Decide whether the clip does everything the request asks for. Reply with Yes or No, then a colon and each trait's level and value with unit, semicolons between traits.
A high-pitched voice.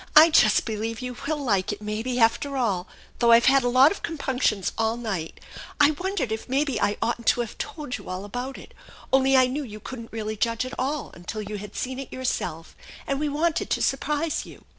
Yes: very high, 250 Hz